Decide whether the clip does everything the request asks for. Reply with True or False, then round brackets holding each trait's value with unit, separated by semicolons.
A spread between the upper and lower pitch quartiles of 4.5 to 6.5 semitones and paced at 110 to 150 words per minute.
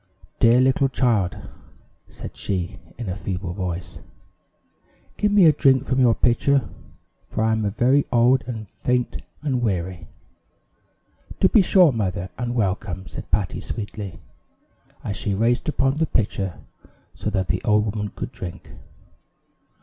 True (5.1 semitones; 140 wpm)